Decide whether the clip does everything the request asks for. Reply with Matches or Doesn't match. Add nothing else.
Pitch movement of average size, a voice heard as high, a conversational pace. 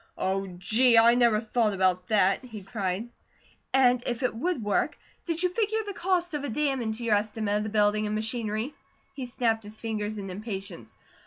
Matches